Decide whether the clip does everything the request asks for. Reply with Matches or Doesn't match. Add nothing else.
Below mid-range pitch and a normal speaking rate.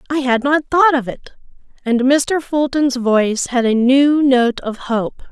Doesn't match